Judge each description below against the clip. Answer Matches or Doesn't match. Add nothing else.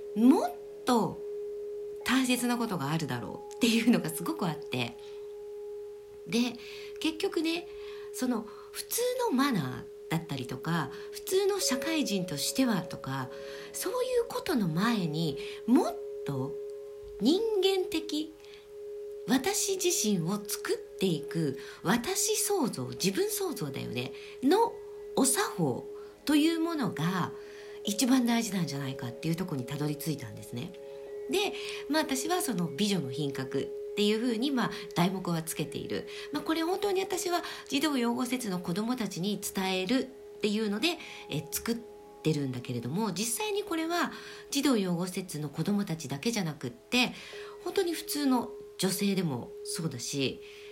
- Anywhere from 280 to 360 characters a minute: Matches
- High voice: Matches